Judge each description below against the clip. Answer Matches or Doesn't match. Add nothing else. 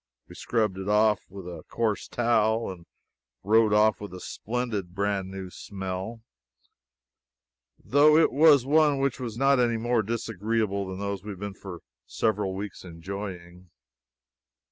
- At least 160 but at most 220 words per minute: Doesn't match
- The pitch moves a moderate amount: Matches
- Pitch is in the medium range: Doesn't match